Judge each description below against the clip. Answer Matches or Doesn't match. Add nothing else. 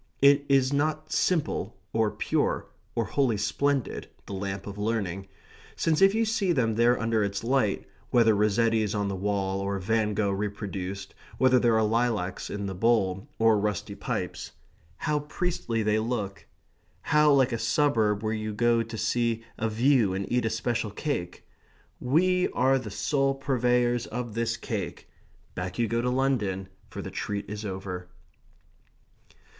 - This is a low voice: Matches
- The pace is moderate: Matches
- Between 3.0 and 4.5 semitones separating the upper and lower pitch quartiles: Matches